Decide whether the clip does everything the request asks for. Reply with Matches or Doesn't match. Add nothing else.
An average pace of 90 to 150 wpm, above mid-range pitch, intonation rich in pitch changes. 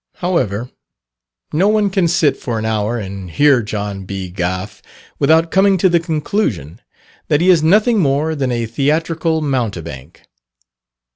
Doesn't match